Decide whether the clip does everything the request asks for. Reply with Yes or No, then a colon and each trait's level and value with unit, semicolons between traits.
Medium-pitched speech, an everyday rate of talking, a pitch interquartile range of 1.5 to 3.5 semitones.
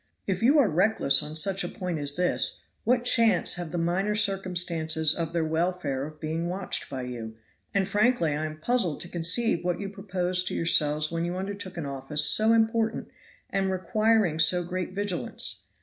No: medium, 180 Hz; average, 180 wpm; average, 4.1 semitones